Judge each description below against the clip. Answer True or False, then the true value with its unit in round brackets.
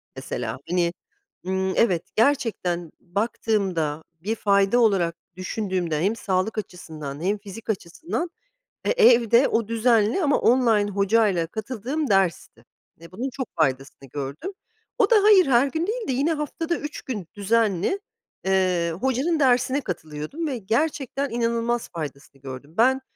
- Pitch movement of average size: False (6.7 semitones)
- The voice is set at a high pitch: True (215 Hz)